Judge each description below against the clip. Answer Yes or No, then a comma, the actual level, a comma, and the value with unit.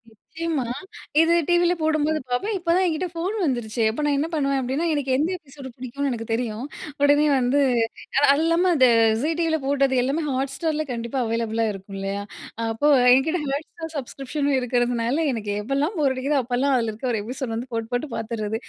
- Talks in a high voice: Yes, very high, 270 Hz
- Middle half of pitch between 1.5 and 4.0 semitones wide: No, average, 4.6 semitones